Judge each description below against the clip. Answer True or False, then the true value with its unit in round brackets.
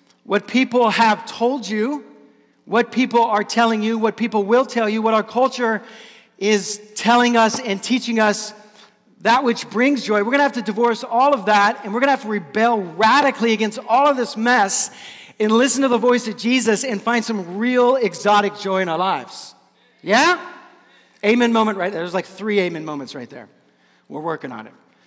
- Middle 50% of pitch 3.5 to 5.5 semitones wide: False (2.7 semitones)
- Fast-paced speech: False (195 wpm)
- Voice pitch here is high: True (225 Hz)